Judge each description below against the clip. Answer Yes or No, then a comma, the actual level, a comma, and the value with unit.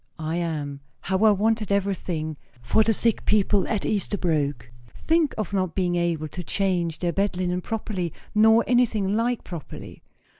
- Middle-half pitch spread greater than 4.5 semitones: No, average, 3.9 semitones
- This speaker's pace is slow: No, average, 155 wpm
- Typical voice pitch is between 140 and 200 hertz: Yes, high, 190 Hz